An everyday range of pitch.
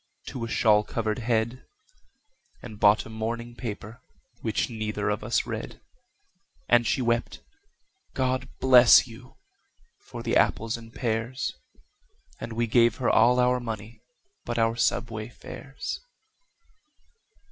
No: narrow, 1.7 semitones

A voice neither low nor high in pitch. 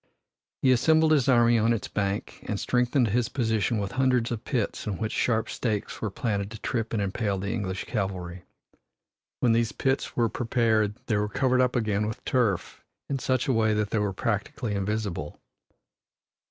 No: low, 110 Hz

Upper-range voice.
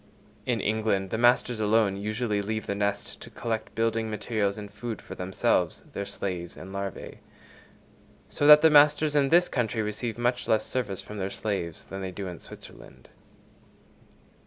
No: low, 110 Hz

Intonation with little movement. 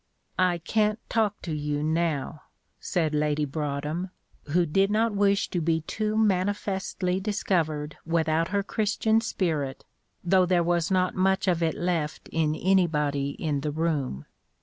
No: average, 4.1 semitones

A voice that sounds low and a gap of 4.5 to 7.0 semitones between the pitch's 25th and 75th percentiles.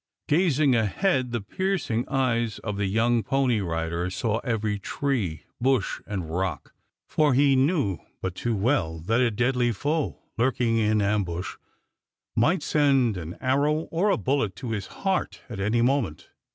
Yes: low, 120 Hz; average, 5.3 semitones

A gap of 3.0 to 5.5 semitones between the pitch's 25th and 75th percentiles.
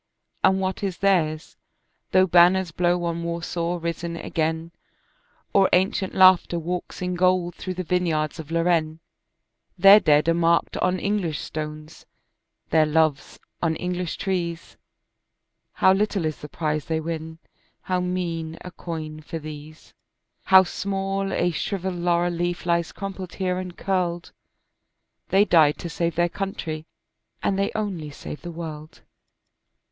No: narrow, 2.4 semitones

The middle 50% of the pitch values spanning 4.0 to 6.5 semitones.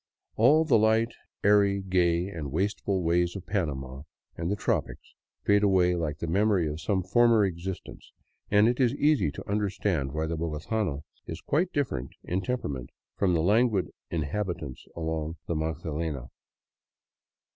Yes: average, 4.6 semitones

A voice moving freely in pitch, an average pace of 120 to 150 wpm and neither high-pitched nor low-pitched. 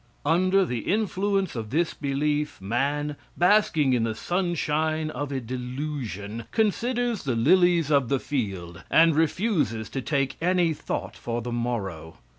Yes: wide, 6.4 semitones; average, 140 wpm; medium, 145 Hz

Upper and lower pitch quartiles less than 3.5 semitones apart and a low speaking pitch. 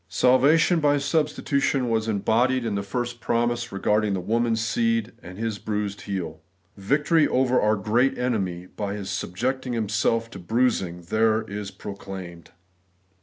No: average, 3.9 semitones; low, 110 Hz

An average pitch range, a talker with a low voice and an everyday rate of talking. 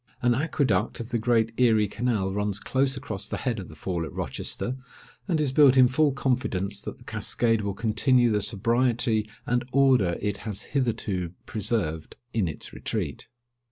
Yes: average, 4.0 semitones; low, 115 Hz; average, 170 wpm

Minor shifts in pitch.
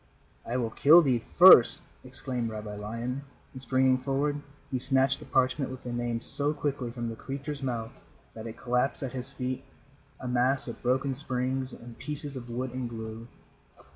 Yes: narrow, 2.2 semitones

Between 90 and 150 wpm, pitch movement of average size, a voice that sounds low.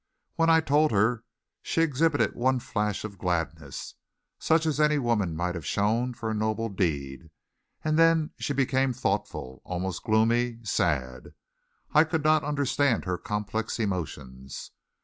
No: average, 145 wpm; wide, 8.0 semitones; low, 115 Hz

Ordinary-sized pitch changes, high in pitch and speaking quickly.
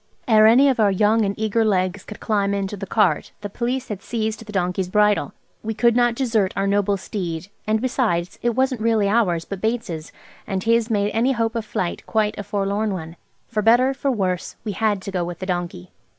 Yes: average, 3.0 semitones; high, 210 Hz; fast, 210 wpm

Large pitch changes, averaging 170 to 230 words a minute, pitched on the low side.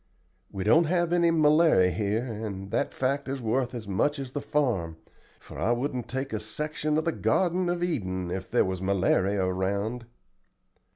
Yes: wide, 7.6 semitones; average, 175 wpm; low, 120 Hz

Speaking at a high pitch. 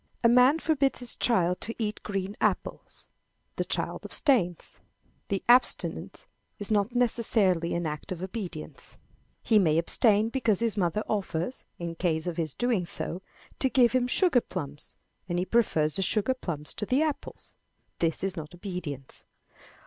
Yes: high, 195 Hz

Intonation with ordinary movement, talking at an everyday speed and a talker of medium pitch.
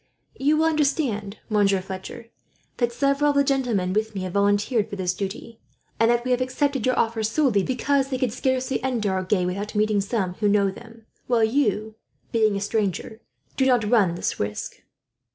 No: average, 4.2 semitones; average, 185 wpm; high, 220 Hz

